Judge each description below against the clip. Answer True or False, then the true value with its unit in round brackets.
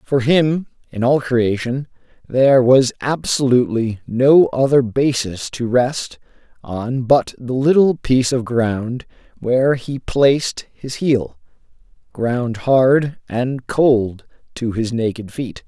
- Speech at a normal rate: False (125 wpm)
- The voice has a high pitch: False (125 Hz)